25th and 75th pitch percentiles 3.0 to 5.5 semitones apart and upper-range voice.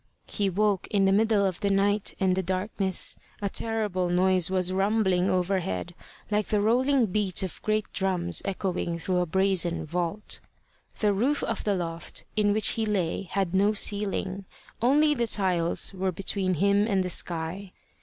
No: narrow, 2.4 semitones; high, 195 Hz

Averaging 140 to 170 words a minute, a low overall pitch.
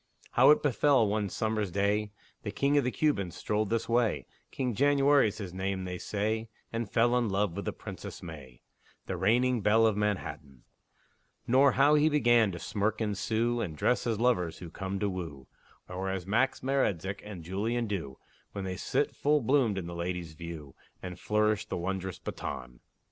No: average, 180 wpm; low, 105 Hz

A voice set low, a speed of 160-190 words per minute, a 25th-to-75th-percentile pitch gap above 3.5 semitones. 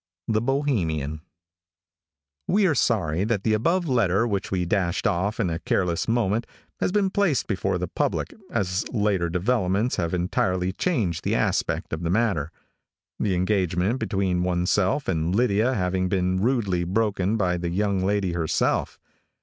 No: very low, 95 Hz; average, 150 wpm; average, 4.0 semitones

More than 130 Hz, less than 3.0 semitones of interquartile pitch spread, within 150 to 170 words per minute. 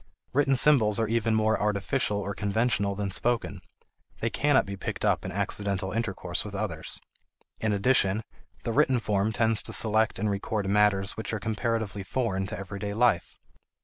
No: low, 105 Hz; narrow, 2.4 semitones; average, 165 wpm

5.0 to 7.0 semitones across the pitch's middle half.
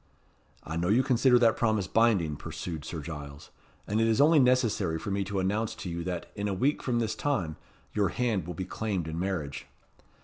Yes: average, 5.3 semitones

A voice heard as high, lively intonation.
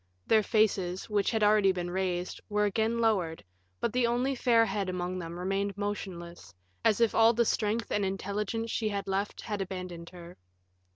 No: high, 200 Hz; average, 3.3 semitones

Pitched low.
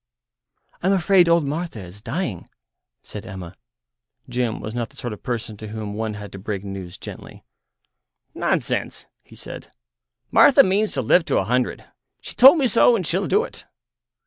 Yes: low, 120 Hz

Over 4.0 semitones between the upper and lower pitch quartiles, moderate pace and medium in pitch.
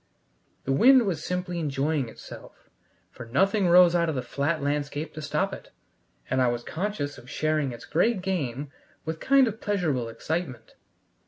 Yes: average, 4.8 semitones; average, 170 wpm; medium, 155 Hz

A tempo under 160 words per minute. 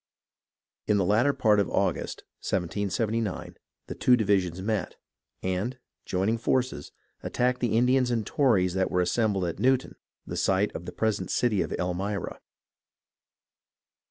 Yes: average, 140 wpm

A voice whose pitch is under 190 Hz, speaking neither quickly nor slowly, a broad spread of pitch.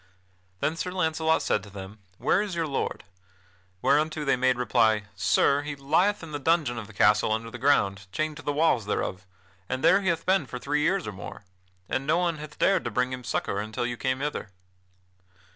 No: medium, 140 Hz; fast, 210 wpm; wide, 6.3 semitones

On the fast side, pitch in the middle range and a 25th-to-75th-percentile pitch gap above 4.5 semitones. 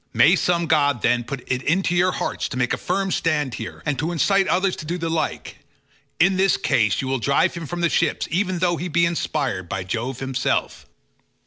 Yes: fast, 215 wpm; medium, 160 Hz; average, 5.2 semitones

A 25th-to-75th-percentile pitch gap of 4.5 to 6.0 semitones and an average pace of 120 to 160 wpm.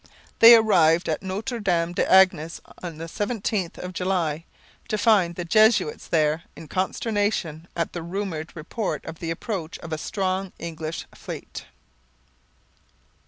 No: average, 3.8 semitones; average, 140 wpm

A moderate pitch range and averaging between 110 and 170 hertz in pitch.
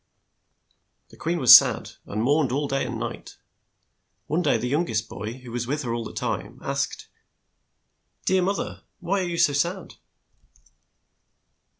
No: wide, 6.4 semitones; medium, 140 Hz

